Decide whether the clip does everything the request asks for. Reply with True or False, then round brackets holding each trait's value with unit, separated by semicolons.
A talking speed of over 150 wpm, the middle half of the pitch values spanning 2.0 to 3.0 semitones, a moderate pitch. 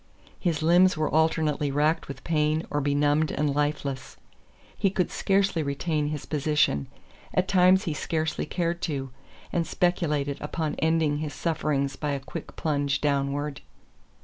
False (145 wpm; 2.4 semitones; 150 Hz)